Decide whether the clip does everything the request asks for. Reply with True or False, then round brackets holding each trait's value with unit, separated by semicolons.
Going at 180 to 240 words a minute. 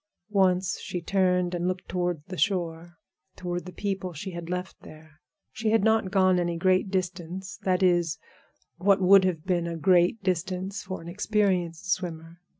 False (160 wpm)